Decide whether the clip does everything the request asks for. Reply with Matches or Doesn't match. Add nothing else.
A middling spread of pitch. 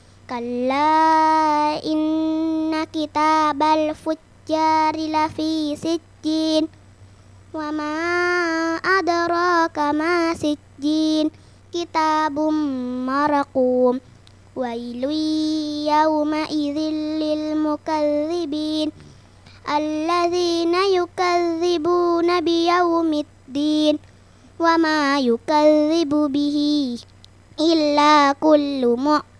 Doesn't match